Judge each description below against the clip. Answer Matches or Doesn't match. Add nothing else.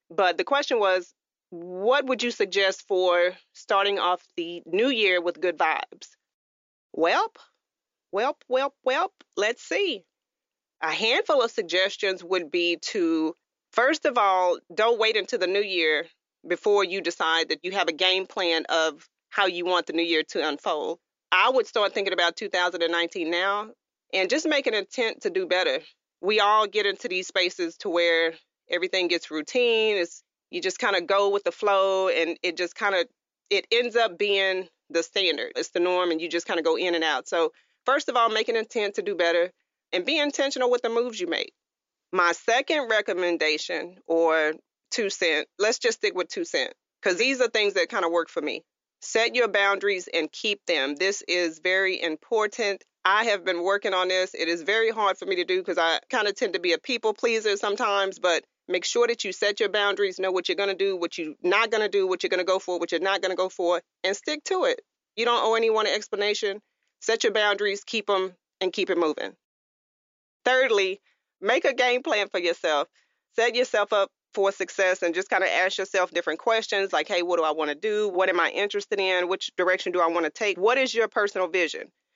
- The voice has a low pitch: Doesn't match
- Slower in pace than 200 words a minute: Doesn't match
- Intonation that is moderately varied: Matches